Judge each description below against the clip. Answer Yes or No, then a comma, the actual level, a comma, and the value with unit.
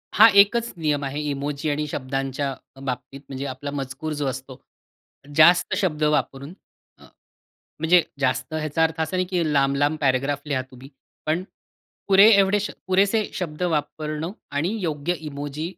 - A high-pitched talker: No, medium, 150 Hz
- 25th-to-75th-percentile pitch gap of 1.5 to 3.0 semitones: No, average, 3.7 semitones